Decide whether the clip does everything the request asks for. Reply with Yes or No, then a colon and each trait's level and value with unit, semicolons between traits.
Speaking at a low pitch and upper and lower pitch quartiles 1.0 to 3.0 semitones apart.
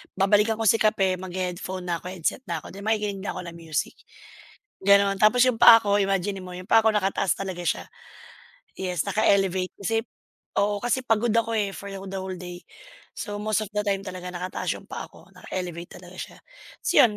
No: high, 195 Hz; narrow, 2.4 semitones